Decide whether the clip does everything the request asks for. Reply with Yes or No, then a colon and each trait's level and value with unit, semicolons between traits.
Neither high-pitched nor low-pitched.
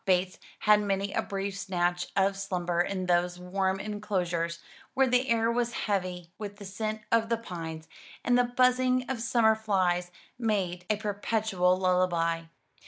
No: high, 195 Hz